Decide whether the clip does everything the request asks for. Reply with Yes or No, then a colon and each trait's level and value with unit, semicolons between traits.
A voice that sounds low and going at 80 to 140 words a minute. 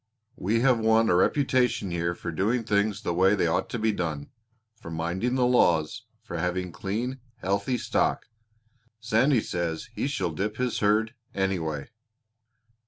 No: low, 100 Hz; average, 155 wpm